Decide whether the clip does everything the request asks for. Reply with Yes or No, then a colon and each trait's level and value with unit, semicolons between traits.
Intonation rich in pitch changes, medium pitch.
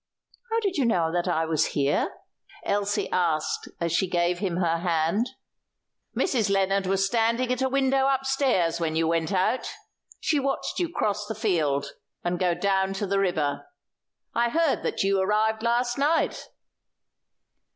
No: wide, 5.9 semitones; high, 195 Hz